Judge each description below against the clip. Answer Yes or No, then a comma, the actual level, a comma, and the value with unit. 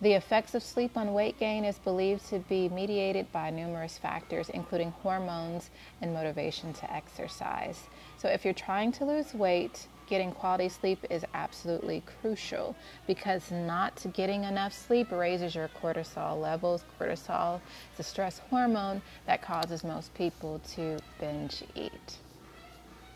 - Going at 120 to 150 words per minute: Yes, average, 145 wpm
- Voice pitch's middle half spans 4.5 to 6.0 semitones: No, average, 3.0 semitones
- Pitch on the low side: No, medium, 185 Hz